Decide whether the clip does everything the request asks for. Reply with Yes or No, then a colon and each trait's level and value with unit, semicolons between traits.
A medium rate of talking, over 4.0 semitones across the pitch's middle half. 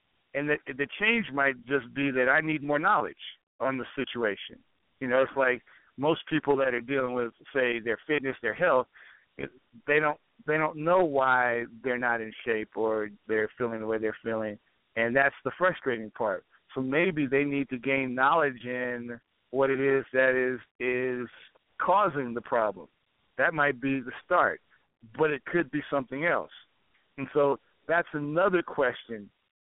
No: average, 170 wpm; average, 3.2 semitones